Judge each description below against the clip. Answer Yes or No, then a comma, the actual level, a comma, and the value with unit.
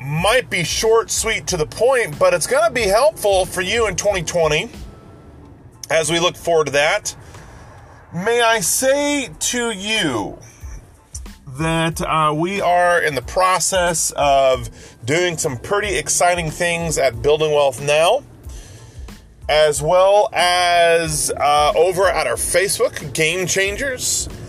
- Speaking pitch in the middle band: Yes, medium, 170 Hz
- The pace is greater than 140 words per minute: No, slow, 135 wpm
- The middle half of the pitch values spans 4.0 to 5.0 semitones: Yes, average, 4.7 semitones